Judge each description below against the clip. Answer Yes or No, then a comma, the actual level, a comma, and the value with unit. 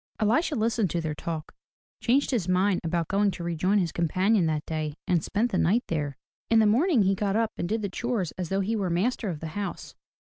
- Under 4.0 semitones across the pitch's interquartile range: No, average, 4.6 semitones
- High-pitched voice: Yes, high, 195 Hz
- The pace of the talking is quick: Yes, fast, 225 wpm